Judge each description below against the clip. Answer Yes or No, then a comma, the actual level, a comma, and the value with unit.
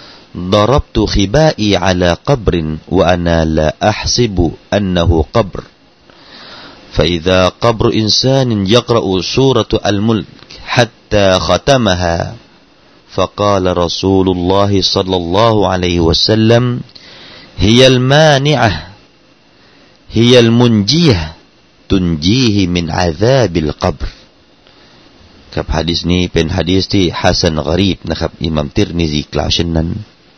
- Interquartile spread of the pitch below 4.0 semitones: No, average, 4.4 semitones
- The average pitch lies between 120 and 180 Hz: No, very low, 95 Hz